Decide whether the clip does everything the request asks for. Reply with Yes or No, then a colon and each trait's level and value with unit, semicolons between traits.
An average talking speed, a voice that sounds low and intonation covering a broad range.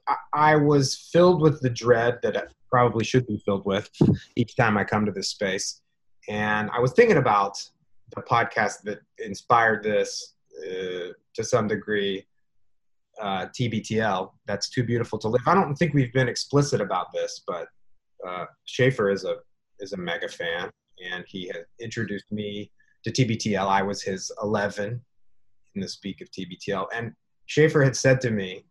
Yes: average, 165 wpm; low, 120 Hz; wide, 6.6 semitones